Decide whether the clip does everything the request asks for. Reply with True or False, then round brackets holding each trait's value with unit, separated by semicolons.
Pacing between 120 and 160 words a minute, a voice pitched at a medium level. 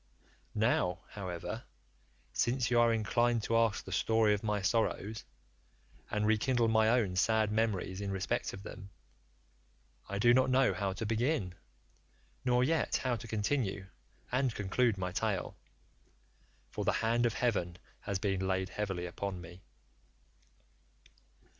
False (140 wpm; 110 Hz)